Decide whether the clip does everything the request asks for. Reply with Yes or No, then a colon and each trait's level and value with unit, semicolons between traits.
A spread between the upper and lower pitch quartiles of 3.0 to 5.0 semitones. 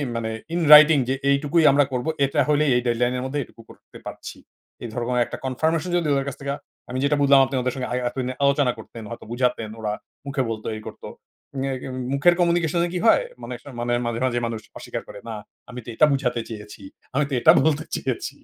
Yes: average, 3.4 semitones